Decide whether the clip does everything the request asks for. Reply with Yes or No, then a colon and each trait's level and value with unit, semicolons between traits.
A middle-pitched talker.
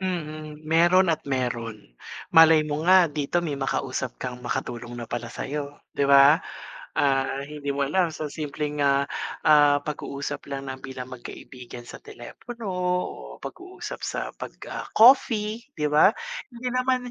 Yes: medium, 145 Hz